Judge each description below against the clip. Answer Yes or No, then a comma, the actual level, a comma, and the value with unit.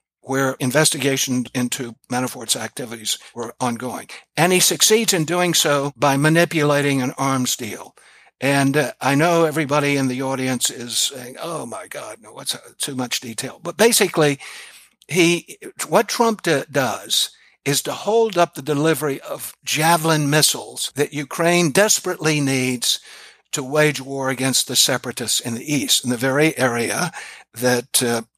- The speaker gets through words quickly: No, average, 150 wpm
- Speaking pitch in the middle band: Yes, medium, 145 Hz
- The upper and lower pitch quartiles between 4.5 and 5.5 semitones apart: No, average, 4.0 semitones